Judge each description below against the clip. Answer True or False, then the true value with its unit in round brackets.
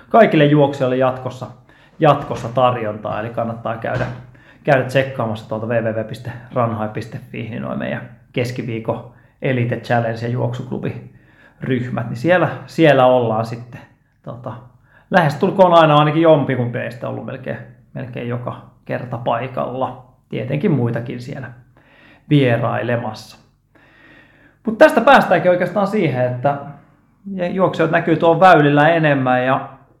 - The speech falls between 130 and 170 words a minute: False (105 wpm)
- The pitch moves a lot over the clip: False (3.7 semitones)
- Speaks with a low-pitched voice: True (130 Hz)